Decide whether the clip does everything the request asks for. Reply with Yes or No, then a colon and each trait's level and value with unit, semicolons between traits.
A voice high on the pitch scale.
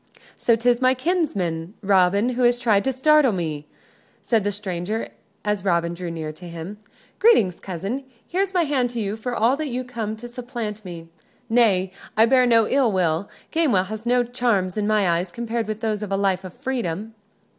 Yes: high, 215 Hz